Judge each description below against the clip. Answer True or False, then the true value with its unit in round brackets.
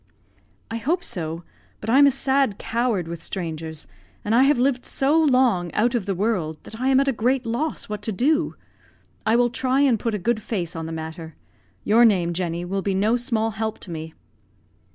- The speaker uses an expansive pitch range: True (6.2 semitones)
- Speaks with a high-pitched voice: True (220 Hz)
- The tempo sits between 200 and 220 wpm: True (205 wpm)